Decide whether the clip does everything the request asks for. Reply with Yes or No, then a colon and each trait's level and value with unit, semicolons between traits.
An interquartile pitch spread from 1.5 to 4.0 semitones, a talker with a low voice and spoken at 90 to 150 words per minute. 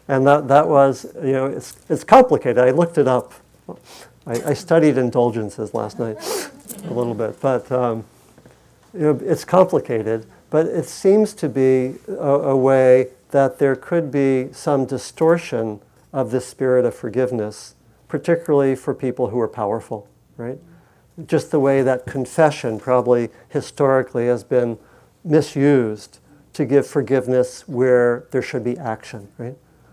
Yes: average, 2.8 semitones; low, 130 Hz; average, 145 wpm